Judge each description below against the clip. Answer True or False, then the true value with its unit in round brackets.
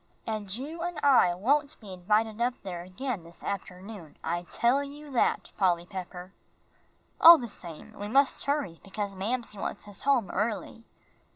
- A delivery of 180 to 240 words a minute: False (160 wpm)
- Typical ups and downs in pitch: False (6.1 semitones)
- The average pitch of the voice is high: True (210 Hz)